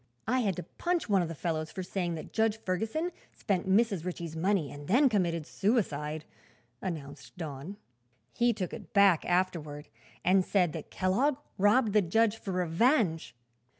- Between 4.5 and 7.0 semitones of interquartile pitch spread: Yes, average, 4.8 semitones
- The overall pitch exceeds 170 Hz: Yes, medium, 185 Hz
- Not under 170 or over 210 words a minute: No, average, 160 wpm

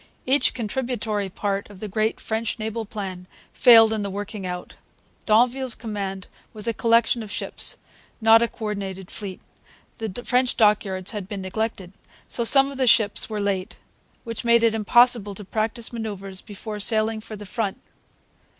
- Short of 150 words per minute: No, average, 165 wpm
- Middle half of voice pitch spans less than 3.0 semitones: Yes, narrow, 2.5 semitones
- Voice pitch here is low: No, high, 215 Hz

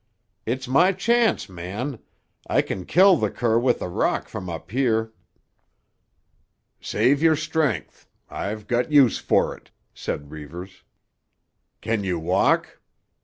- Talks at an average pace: No, slow, 125 wpm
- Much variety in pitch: Yes, wide, 7.6 semitones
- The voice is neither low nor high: No, low, 115 Hz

